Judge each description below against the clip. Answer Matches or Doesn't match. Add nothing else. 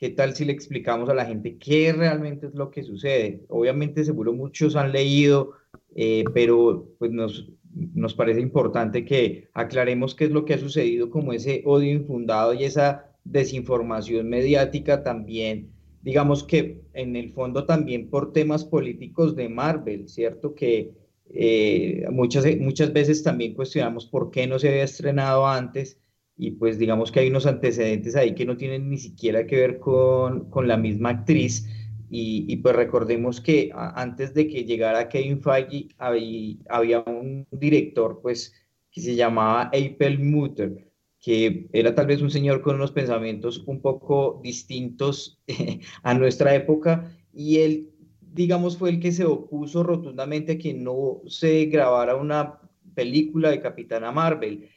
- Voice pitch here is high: Doesn't match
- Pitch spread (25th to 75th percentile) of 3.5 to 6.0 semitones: Matches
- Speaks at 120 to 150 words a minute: Doesn't match